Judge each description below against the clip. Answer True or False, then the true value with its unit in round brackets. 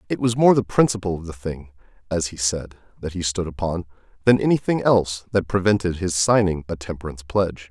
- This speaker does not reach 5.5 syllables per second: False (6.0 syllables/s)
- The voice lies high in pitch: False (90 Hz)